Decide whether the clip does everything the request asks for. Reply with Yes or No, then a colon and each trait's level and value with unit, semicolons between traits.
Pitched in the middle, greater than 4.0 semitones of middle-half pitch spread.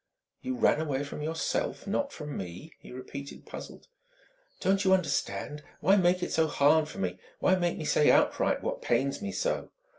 Yes: medium, 160 Hz; average, 5.0 semitones